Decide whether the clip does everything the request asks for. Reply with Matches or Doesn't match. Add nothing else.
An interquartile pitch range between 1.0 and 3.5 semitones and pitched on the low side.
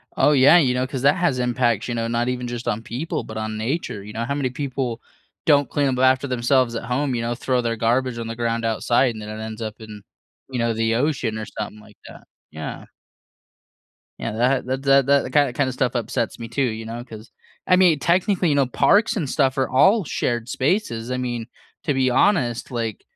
Matches